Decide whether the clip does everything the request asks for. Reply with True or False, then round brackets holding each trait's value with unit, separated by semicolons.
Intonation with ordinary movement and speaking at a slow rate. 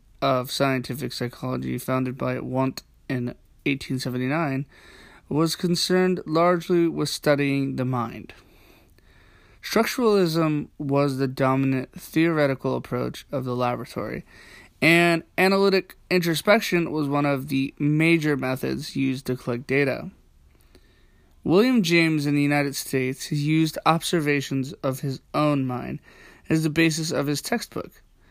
True (4.1 semitones; 115 wpm)